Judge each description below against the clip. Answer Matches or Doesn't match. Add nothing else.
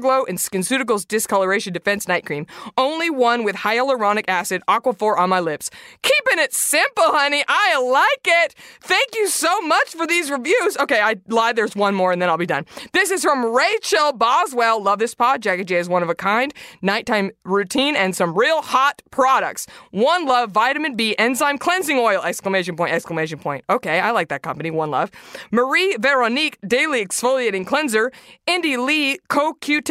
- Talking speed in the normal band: Matches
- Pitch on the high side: Matches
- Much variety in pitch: Matches